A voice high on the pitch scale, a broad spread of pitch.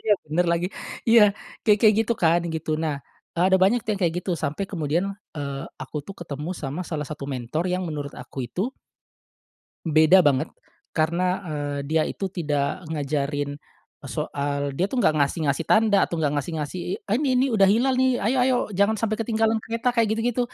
No: medium, 165 Hz; wide, 6.4 semitones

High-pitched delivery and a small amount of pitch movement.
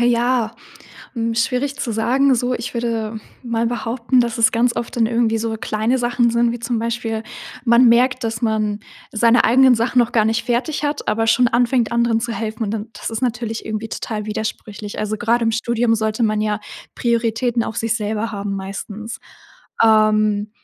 Yes: high, 230 Hz; narrow, 1.6 semitones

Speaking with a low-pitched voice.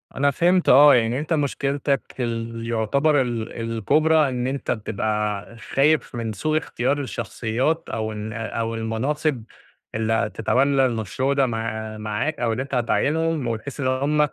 Yes: low, 125 Hz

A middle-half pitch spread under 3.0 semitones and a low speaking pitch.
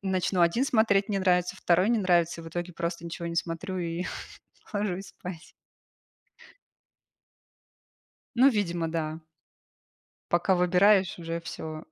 No: narrow, 2.4 semitones; medium, 180 Hz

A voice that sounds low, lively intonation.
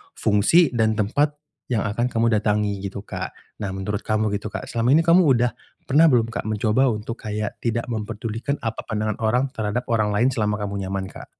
No: low, 110 Hz; average, 2.7 semitones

